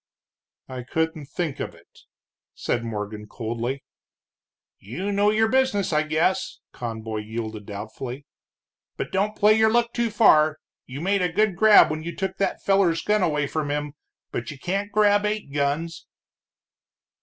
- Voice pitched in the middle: Yes, medium, 160 Hz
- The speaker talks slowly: No, average, 155 wpm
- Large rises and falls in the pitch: Yes, wide, 7.9 semitones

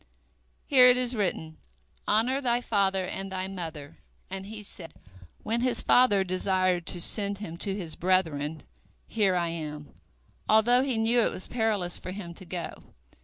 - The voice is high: Yes, high, 195 Hz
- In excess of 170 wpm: No, average, 165 wpm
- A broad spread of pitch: No, average, 4.2 semitones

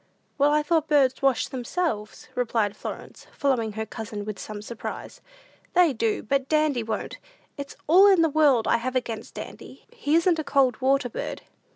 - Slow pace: No, average, 175 wpm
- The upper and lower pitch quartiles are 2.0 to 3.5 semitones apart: No, average, 5.2 semitones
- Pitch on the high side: Yes, very high, 265 Hz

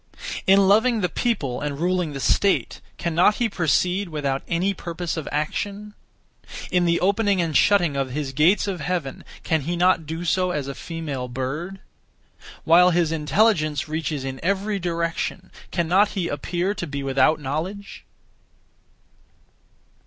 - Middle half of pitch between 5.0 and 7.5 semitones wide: No, average, 4.2 semitones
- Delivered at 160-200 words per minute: No, average, 145 wpm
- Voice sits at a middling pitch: Yes, medium, 170 Hz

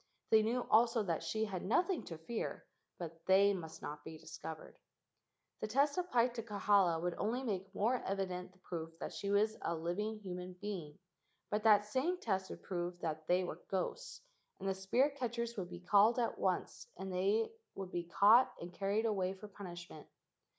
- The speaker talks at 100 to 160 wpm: No, average, 185 wpm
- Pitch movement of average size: Yes, average, 3.8 semitones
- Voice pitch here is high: Yes, high, 195 Hz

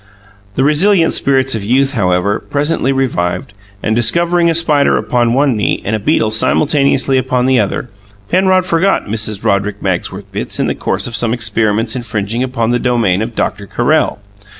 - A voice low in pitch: Yes, low, 120 Hz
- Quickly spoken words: No, average, 170 wpm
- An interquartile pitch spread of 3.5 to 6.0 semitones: Yes, average, 4.8 semitones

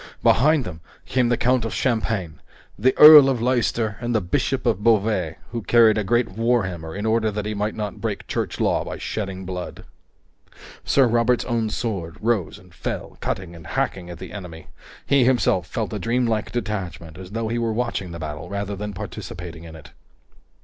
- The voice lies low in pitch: Yes, low, 105 Hz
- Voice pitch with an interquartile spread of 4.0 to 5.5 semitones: Yes, average, 4.5 semitones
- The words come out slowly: No, average, 185 wpm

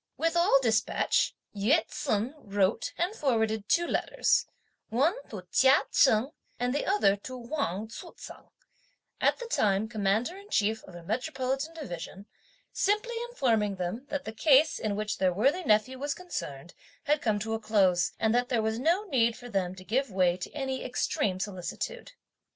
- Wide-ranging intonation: Yes, wide, 5.9 semitones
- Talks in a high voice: Yes, high, 230 Hz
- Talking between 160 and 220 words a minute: Yes, average, 170 wpm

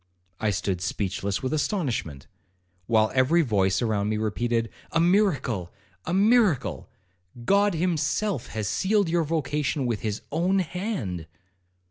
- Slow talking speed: Yes, slow, 120 wpm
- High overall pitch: No, low, 130 Hz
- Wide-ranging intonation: Yes, wide, 8.8 semitones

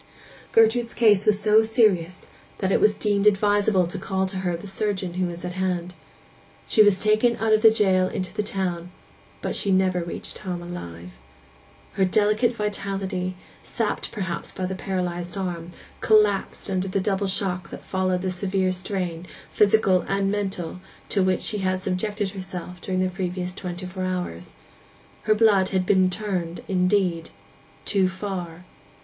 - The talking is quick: No, average, 160 wpm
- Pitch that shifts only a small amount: Yes, narrow, 2.2 semitones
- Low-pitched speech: No, high, 190 Hz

